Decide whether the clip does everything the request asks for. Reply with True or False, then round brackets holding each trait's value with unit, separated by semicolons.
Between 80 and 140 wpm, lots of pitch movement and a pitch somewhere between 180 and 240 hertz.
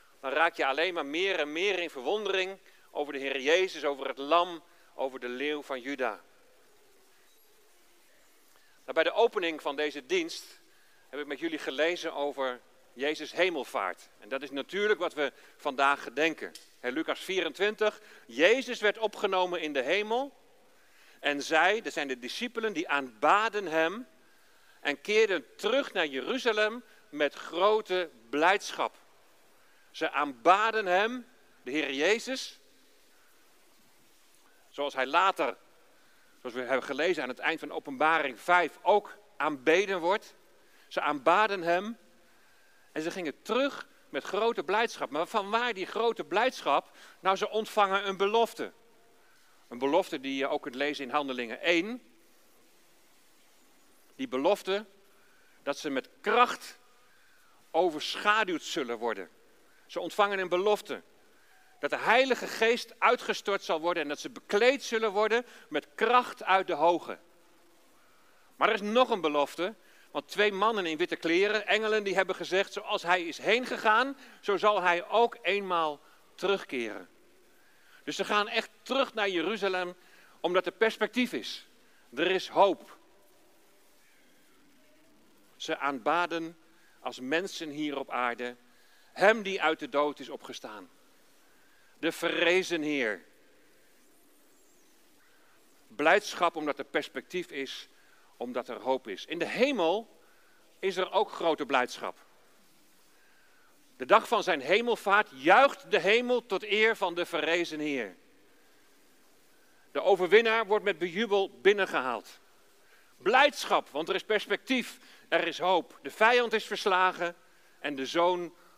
True (135 wpm; 6.5 semitones; 190 Hz)